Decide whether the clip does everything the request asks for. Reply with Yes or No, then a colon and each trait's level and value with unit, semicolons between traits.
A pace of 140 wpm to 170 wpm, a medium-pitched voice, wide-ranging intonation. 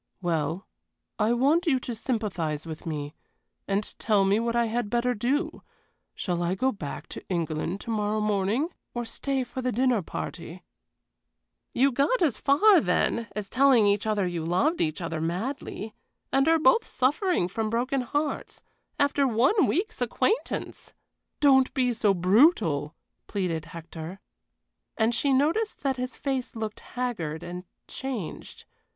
No: average, 150 wpm; high, 225 Hz; wide, 6.8 semitones